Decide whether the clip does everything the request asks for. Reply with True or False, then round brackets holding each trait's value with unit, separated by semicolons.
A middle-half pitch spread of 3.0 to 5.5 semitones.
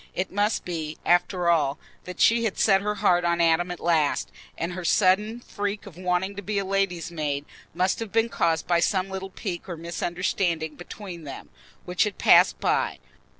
False (2.6 semitones)